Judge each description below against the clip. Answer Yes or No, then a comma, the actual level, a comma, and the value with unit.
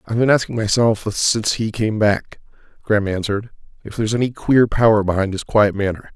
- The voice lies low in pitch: Yes, low, 110 Hz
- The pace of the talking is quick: No, average, 185 wpm